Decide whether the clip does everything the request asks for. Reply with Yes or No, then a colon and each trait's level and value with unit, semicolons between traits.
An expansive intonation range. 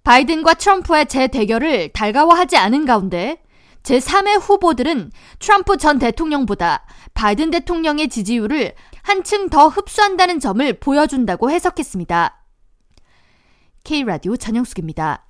Yes: wide, 6.6 semitones